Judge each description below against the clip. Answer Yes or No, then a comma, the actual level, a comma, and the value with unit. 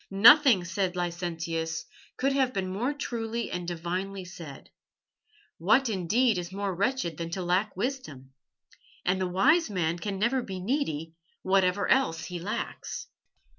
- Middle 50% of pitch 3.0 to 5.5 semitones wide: Yes, average, 5.2 semitones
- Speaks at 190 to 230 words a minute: No, average, 140 wpm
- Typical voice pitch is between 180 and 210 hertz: Yes, high, 190 Hz